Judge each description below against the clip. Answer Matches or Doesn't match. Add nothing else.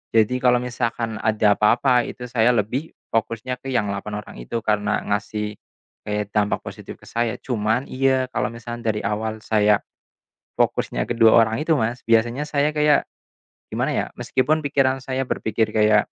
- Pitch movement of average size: Matches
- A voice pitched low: Matches